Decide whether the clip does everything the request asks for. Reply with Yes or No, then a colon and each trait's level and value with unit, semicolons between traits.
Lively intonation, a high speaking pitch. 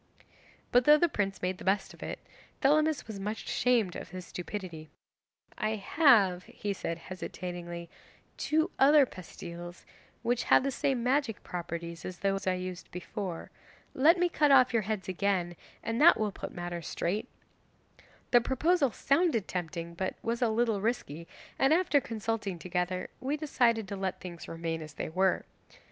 Yes: wide, 6.0 semitones; high, 200 Hz